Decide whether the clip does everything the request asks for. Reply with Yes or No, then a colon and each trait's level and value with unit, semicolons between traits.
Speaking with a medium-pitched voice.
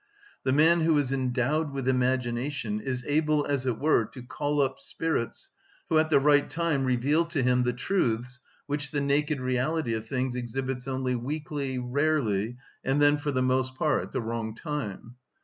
No: low, 130 Hz